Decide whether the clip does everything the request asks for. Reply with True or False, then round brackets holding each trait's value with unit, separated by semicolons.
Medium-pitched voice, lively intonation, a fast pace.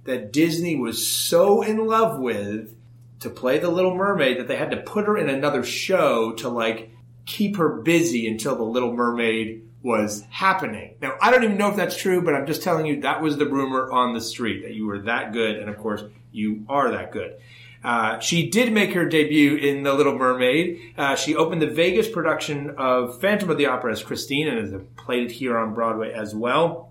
False (130 Hz; 6.3 semitones; 215 wpm)